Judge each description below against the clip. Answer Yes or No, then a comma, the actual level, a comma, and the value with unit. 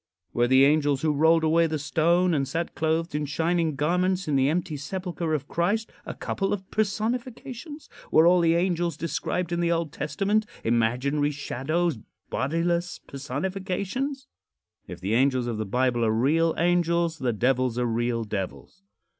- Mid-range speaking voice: Yes, medium, 160 Hz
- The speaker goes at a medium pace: Yes, average, 160 wpm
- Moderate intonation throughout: Yes, average, 4.7 semitones